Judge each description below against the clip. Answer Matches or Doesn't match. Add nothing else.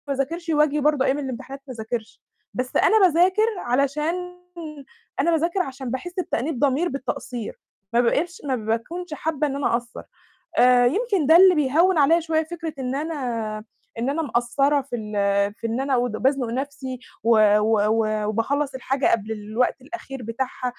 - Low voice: Doesn't match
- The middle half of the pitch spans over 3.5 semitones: Matches